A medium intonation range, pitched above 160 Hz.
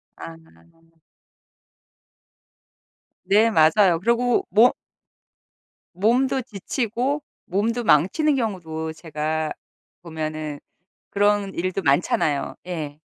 No: wide, 6.4 semitones; medium, 185 Hz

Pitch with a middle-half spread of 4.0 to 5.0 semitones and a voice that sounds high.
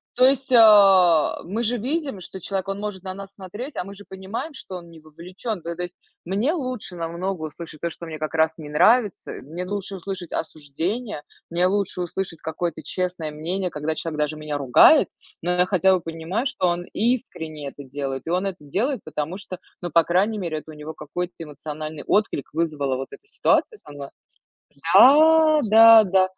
No: average, 4.3 semitones; medium, 180 Hz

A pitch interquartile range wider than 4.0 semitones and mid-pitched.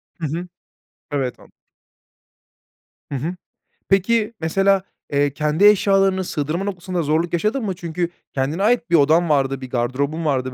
Yes: average, 5.2 semitones; medium, 165 Hz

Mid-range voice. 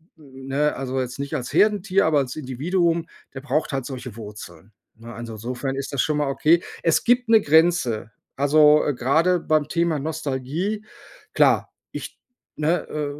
Yes: medium, 145 Hz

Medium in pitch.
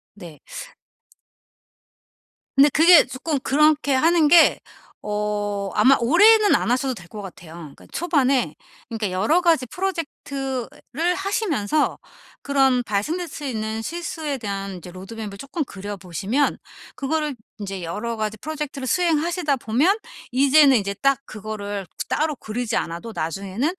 No: very high, 260 Hz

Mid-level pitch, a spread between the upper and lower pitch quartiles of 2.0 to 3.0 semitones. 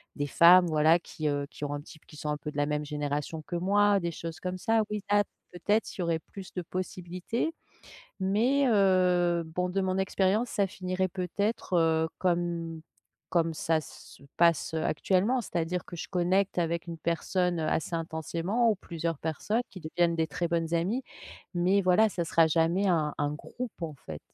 Yes: medium, 175 Hz; average, 2.7 semitones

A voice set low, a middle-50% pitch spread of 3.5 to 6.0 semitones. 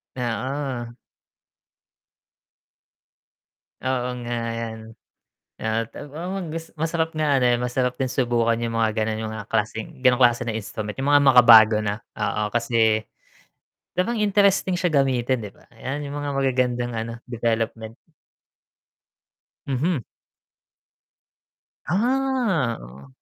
Yes: low, 125 Hz; average, 4.2 semitones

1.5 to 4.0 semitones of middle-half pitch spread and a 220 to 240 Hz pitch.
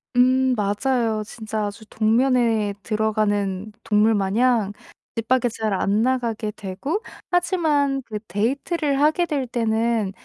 Yes: average, 3.5 semitones; high, 225 Hz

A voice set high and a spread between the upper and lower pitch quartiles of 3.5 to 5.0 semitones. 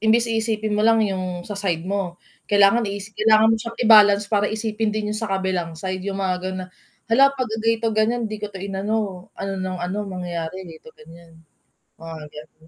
No: high, 200 Hz; average, 2.9 semitones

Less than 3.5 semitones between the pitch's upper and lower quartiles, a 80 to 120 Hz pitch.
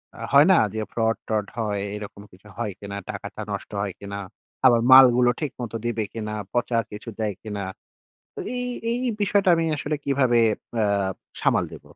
No: average, 4.1 semitones; low, 115 Hz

